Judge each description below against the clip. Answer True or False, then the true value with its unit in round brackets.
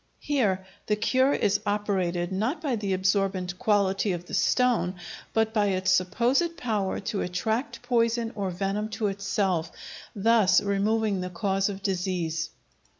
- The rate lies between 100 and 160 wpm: True (145 wpm)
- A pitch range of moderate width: True (3.0 semitones)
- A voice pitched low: False (200 Hz)